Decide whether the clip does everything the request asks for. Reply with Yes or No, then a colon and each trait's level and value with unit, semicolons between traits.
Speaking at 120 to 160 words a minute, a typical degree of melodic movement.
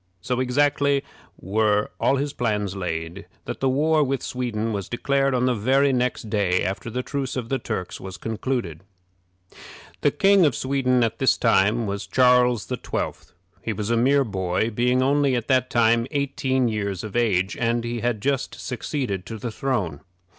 No: average, 175 wpm; average, 4.1 semitones